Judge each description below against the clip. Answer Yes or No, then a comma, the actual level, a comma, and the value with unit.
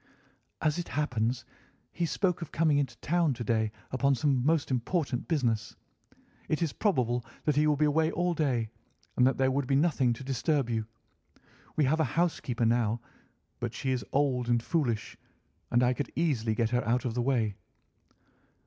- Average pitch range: Yes, average, 4.3 semitones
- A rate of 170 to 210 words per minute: Yes, average, 180 wpm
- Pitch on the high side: No, low, 130 Hz